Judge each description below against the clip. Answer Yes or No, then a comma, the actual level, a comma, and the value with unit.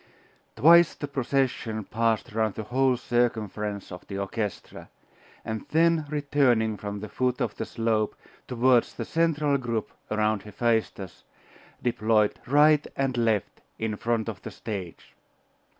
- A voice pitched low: Yes, low, 115 Hz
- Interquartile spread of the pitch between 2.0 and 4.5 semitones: Yes, average, 3.9 semitones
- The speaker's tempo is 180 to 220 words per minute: No, slow, 135 wpm